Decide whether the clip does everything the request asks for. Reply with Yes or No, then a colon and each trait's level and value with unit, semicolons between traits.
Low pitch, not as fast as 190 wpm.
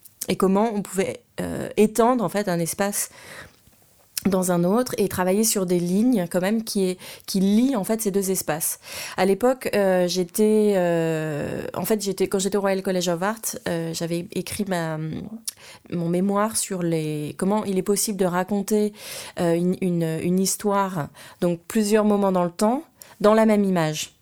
No: high, 190 Hz; average, 180 wpm